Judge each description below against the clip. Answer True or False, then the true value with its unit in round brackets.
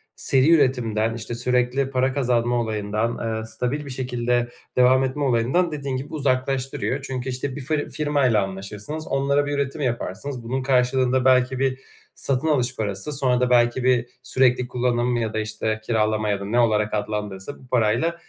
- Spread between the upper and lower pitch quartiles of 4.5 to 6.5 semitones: False (2.8 semitones)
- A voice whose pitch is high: False (125 Hz)